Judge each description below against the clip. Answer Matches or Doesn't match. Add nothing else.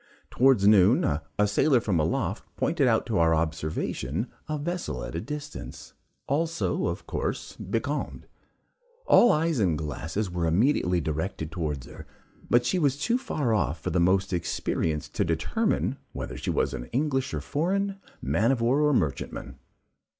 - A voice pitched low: Matches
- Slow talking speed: Doesn't match